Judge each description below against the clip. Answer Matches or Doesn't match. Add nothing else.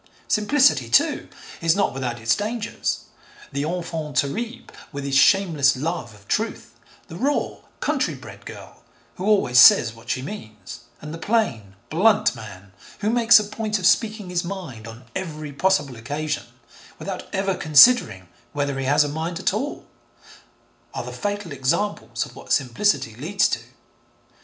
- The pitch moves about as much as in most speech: Doesn't match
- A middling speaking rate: Matches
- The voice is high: Doesn't match